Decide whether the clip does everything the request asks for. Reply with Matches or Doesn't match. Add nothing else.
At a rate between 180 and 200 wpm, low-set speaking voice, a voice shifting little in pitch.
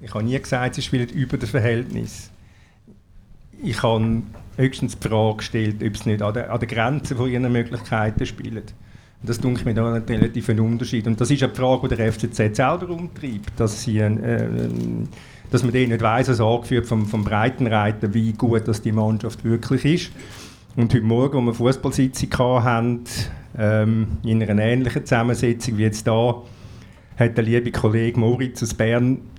Doesn't match